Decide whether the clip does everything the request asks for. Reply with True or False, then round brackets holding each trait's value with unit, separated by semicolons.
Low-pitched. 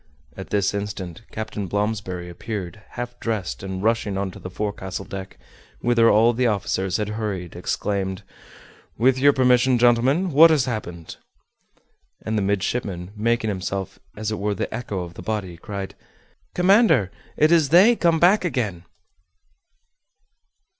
True (105 Hz)